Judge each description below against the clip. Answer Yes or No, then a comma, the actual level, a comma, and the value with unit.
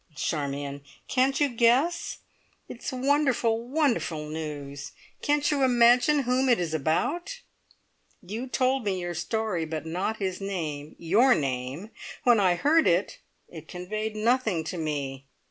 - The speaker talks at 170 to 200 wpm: No, average, 140 wpm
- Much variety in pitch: Yes, wide, 8.2 semitones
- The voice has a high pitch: Yes, high, 210 Hz